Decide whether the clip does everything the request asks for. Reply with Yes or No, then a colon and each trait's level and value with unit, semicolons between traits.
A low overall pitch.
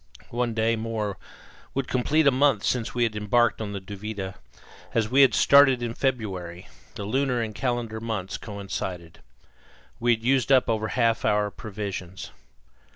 Yes: low, 115 Hz